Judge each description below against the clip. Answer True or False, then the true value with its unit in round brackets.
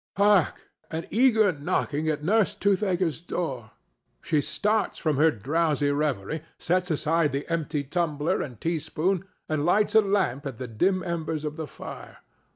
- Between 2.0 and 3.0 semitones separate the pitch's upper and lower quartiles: False (4.0 semitones)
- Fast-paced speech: False (155 wpm)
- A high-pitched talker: False (160 Hz)